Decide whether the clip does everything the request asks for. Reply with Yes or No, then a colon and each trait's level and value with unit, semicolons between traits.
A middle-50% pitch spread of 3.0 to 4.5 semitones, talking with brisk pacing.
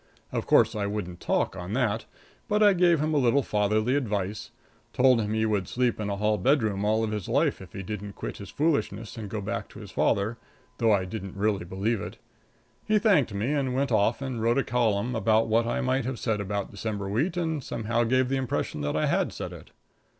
Yes: average, 4.1 semitones; fast, 220 wpm